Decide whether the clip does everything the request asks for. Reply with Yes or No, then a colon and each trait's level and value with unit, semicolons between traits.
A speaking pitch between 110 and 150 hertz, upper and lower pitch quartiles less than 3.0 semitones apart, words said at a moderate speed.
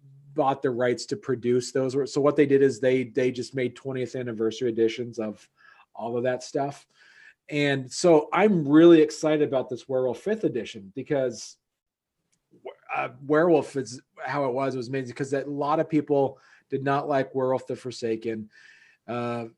Yes: low, 135 Hz; narrow, 2.5 semitones; average, 170 wpm